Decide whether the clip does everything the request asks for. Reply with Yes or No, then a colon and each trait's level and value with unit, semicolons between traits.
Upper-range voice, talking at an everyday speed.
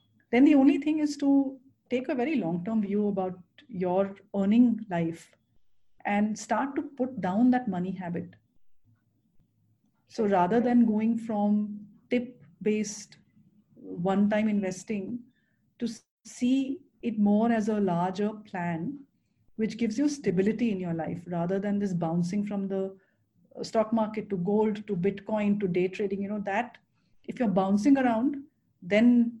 Yes: high, 210 Hz; average, 145 wpm